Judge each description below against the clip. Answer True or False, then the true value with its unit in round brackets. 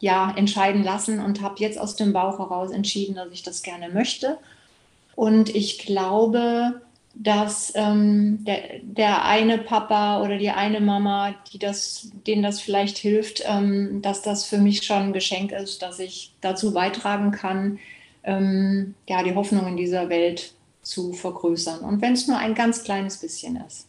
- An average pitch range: False (1.7 semitones)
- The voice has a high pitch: True (200 Hz)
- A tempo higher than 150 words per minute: True (170 wpm)